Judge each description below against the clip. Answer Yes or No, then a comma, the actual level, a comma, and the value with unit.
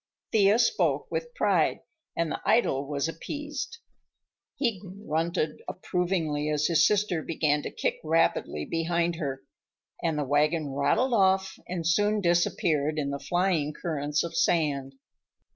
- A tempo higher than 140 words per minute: No, slow, 135 wpm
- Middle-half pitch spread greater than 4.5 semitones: No, average, 4.2 semitones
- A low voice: No, medium, 165 Hz